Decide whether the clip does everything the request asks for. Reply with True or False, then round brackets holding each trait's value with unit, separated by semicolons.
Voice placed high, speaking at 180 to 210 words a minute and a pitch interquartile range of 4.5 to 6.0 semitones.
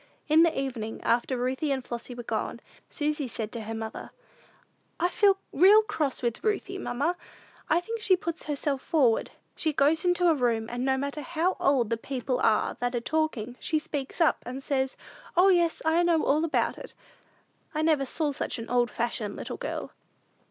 True (280 Hz; 185 wpm; 5.1 semitones)